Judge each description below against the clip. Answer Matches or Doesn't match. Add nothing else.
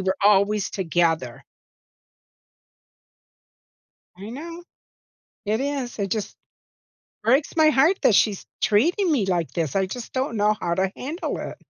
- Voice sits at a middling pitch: Doesn't match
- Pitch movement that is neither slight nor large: Doesn't match